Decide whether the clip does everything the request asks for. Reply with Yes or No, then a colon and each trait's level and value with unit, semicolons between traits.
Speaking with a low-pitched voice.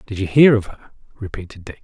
Yes: low, 105 Hz